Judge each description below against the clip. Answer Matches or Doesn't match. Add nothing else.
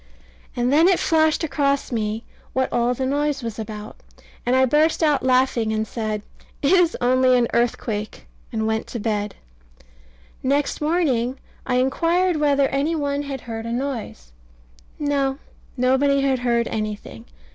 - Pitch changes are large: Doesn't match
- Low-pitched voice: Doesn't match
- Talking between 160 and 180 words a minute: Doesn't match